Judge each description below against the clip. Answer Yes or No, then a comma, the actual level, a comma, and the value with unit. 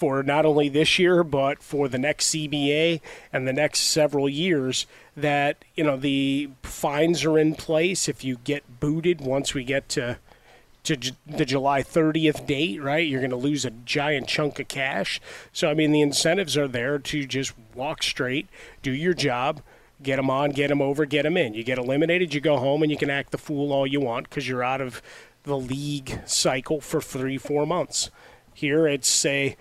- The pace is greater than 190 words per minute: Yes, average, 200 wpm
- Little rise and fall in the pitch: Yes, narrow, 2.3 semitones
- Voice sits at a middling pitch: Yes, medium, 145 Hz